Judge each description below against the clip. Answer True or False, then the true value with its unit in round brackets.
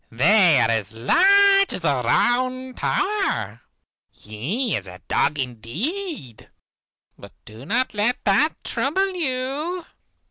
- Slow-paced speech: True (115 wpm)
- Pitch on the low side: False (240 Hz)